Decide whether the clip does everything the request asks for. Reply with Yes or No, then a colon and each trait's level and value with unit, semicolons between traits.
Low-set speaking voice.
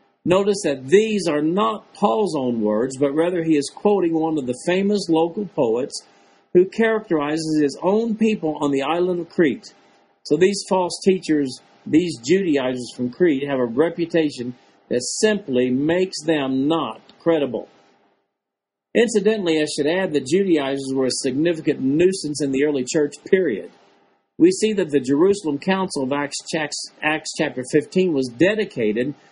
No: medium, 155 Hz